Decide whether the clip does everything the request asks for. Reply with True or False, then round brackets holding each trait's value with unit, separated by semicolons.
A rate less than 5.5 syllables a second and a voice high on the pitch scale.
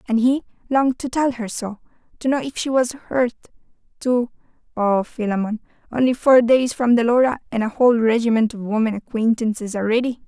False (5.7 syllables/s; 235 Hz)